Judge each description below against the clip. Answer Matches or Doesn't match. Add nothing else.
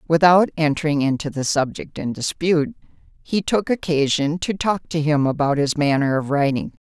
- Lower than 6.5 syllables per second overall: Matches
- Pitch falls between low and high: Matches